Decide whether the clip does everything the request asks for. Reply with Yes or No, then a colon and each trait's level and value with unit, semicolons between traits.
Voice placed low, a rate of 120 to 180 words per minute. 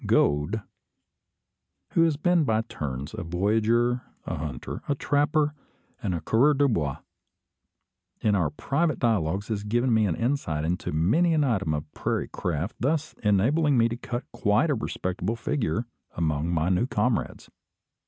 Yes: low, 110 Hz; average, 155 wpm